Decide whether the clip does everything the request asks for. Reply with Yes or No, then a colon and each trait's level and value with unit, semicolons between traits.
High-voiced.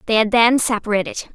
Yes: high, 220 Hz